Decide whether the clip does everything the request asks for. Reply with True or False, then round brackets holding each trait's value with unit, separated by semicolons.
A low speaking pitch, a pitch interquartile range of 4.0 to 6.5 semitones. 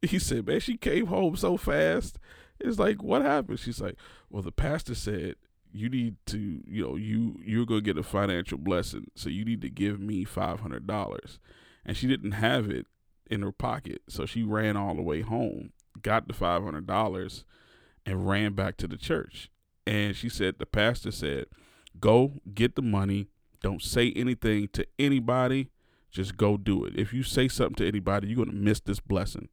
False (105 Hz; 3.3 semitones)